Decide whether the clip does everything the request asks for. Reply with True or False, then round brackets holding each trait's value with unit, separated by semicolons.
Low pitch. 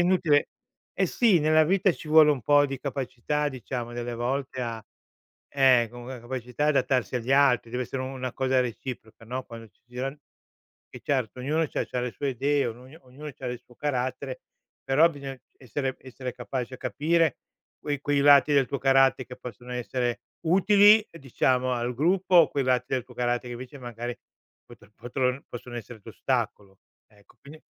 True (130 Hz)